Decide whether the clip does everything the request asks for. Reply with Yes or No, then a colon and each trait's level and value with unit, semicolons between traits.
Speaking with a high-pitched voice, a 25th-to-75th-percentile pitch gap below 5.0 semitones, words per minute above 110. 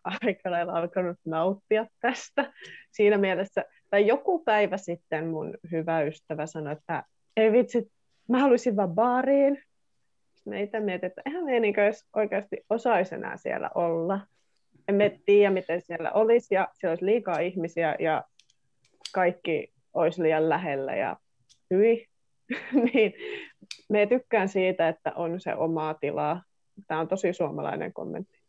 No: high, 195 Hz; average, 5.3 semitones; average, 130 wpm